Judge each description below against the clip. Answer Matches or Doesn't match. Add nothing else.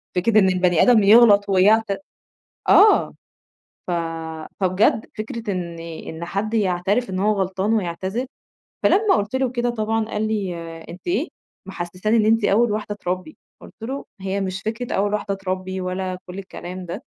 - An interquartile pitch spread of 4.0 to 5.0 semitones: Doesn't match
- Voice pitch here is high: Matches